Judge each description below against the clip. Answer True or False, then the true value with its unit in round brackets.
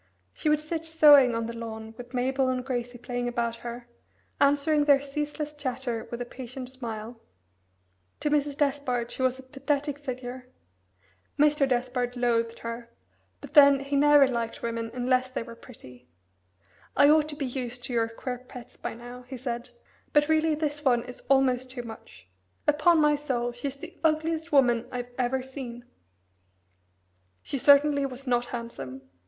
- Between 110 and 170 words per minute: True (165 wpm)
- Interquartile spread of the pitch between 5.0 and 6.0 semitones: False (3.1 semitones)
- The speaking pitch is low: False (255 Hz)